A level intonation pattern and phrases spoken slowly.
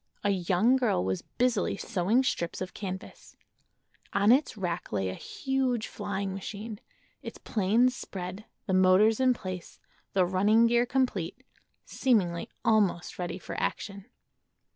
No: average, 4.2 semitones; slow, 125 wpm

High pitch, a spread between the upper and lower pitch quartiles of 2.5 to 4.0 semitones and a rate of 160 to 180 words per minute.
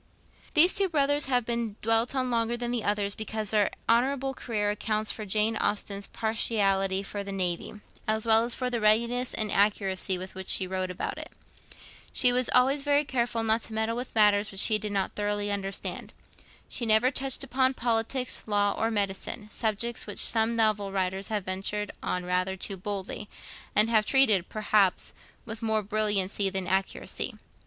Yes: high, 215 Hz; average, 2.9 semitones; average, 175 wpm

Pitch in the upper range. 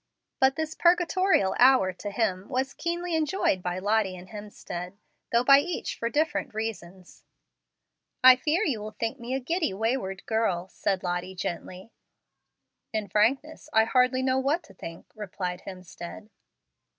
Yes: high, 225 Hz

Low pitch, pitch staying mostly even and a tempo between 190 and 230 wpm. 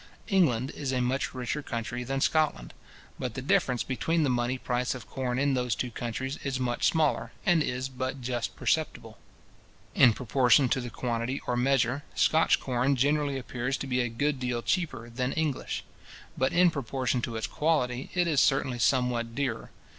No: low, 130 Hz; narrow, 2.3 semitones; average, 175 wpm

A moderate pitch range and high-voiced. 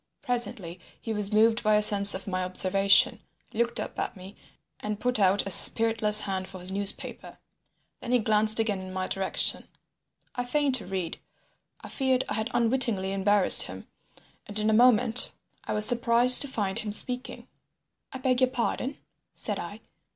Yes: average, 3.7 semitones; high, 215 Hz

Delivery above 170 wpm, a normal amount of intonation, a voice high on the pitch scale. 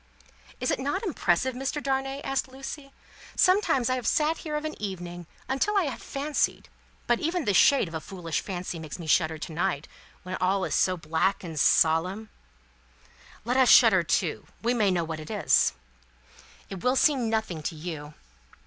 No: average, 185 wpm; wide, 8.1 semitones; high, 200 Hz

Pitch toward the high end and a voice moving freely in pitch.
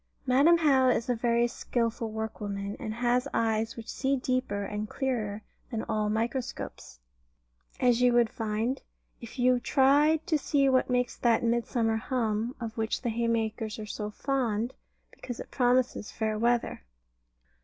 No: high, 235 Hz; narrow, 2.5 semitones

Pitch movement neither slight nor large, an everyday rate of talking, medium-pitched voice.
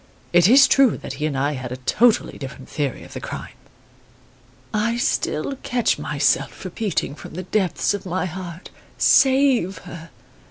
No: wide, 7.4 semitones; average, 160 wpm; medium, 180 Hz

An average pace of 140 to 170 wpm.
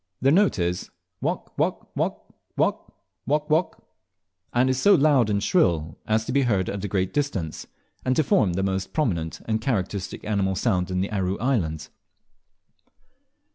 Yes: average, 160 wpm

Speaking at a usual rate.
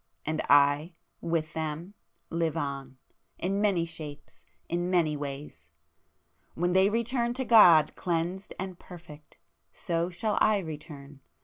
No: slow, 120 wpm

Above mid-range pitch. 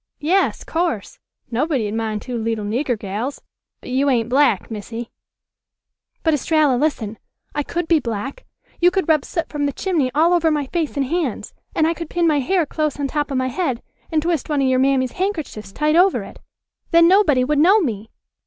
Yes: very high, 290 Hz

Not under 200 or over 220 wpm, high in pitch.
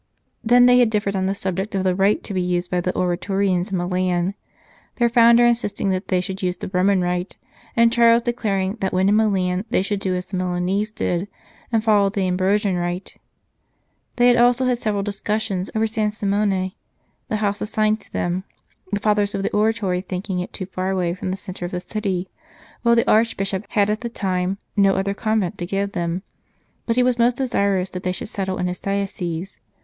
Yes: fast, 205 wpm; high, 195 Hz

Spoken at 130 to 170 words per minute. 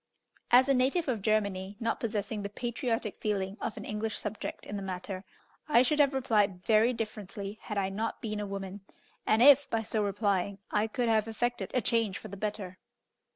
No: average, 195 wpm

